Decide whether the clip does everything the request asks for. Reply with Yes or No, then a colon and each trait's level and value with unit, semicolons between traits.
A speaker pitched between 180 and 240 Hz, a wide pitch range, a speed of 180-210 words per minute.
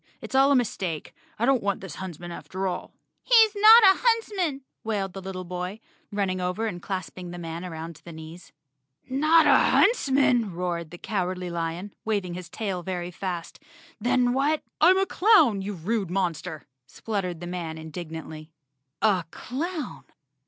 No: high, 190 Hz; wide, 6.4 semitones; average, 160 wpm